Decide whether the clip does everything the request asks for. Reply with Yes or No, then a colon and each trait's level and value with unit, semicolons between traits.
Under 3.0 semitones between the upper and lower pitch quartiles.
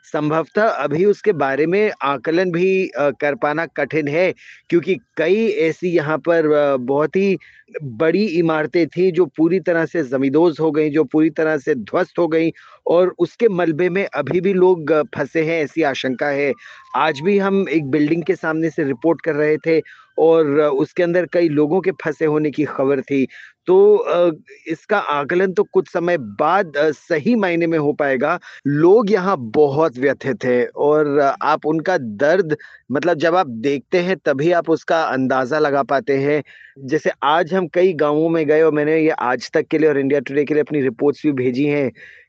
No: average, 3.5 semitones